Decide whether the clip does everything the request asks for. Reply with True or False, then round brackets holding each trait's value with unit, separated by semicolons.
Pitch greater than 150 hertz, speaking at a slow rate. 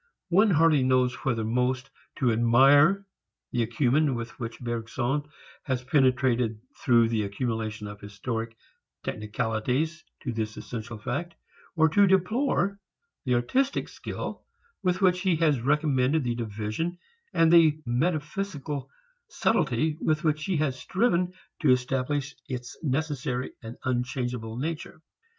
False (130 Hz; 125 wpm)